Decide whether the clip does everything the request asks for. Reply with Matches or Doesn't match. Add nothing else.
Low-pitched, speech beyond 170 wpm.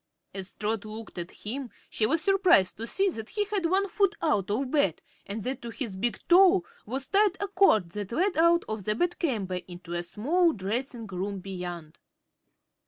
Doesn't match